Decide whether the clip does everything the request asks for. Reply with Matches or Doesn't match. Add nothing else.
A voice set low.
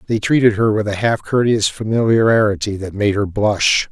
Matches